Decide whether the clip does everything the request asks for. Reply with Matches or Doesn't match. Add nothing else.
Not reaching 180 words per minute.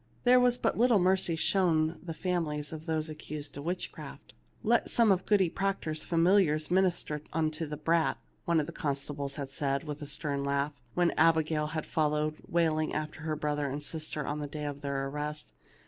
Doesn't match